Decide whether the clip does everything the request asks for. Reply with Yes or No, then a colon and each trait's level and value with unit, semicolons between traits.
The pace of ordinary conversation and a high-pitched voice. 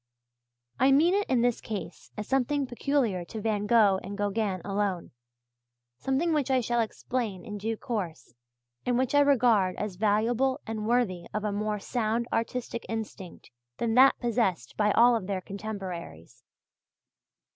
Yes: average, 150 wpm; high, 220 Hz